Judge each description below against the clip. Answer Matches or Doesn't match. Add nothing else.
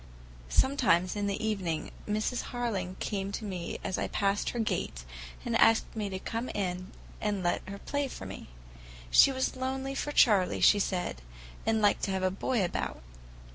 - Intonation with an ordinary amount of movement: Matches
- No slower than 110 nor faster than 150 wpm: Doesn't match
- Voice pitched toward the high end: Matches